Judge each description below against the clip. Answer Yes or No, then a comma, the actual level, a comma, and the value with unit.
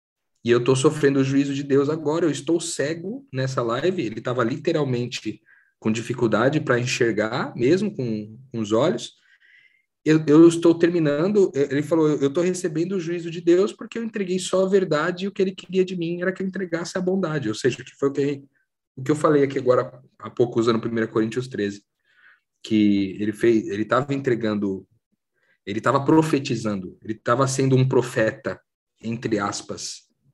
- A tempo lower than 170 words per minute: No, fast, 185 wpm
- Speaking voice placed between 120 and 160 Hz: Yes, medium, 140 Hz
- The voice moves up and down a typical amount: No, wide, 6.7 semitones